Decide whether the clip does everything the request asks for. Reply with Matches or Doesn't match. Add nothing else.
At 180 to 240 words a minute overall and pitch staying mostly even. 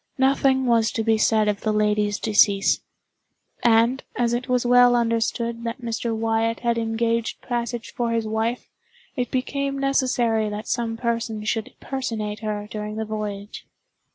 Doesn't match